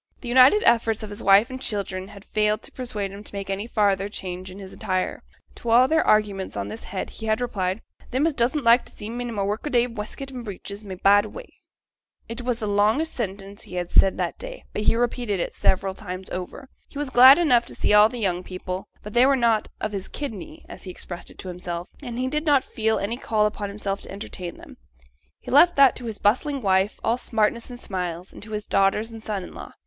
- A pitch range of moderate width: Yes, average, 3.8 semitones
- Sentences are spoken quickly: Yes, fast, 235 wpm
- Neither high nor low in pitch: No, high, 210 Hz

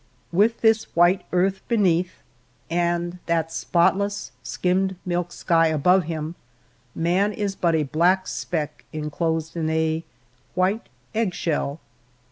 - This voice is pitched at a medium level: Yes, medium, 175 Hz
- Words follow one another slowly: Yes, slow, 120 wpm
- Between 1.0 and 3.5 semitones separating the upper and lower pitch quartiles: Yes, average, 2.8 semitones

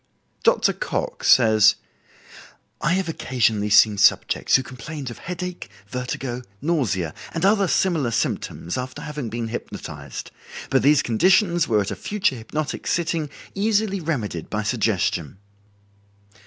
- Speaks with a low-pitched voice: Yes, low, 130 Hz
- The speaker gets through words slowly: Yes, slow, 130 wpm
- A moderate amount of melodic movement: No, wide, 7.3 semitones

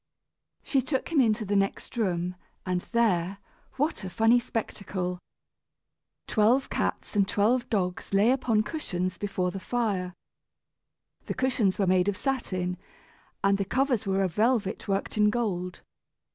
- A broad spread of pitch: No, average, 4.3 semitones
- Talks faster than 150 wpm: No, average, 145 wpm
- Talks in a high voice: Yes, high, 205 Hz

